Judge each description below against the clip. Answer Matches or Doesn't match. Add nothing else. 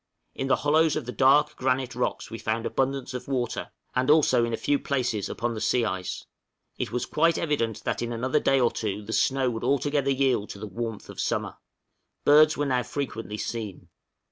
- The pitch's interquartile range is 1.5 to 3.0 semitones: Doesn't match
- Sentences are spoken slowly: Doesn't match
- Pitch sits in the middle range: Doesn't match